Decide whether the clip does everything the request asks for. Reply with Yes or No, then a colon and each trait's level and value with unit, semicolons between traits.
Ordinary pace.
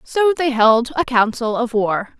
Yes: average, 190 wpm